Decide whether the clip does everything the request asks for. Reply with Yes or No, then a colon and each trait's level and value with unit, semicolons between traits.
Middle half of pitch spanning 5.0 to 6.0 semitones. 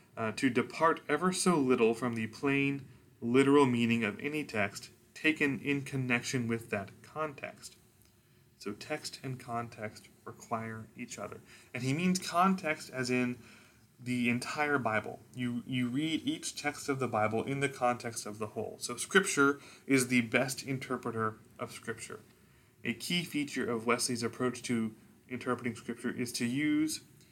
No: average, 3.2 semitones